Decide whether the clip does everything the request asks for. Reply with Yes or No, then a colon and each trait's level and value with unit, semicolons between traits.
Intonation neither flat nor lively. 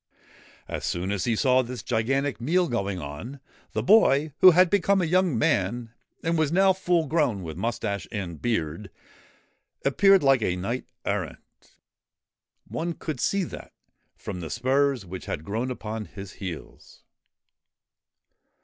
No: wide, 8.0 semitones